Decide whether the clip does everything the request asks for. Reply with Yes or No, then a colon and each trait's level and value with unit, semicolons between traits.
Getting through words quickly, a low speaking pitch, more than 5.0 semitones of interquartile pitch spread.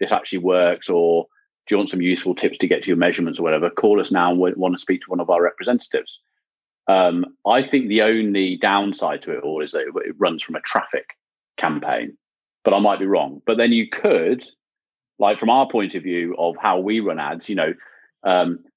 Yes: fast, 225 wpm; low, 100 Hz; wide, 5.6 semitones